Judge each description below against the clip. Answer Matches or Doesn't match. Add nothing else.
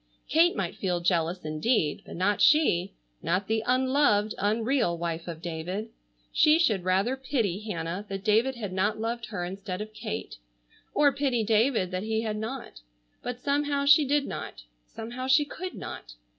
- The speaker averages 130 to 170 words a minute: Matches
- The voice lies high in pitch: Matches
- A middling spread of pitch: Doesn't match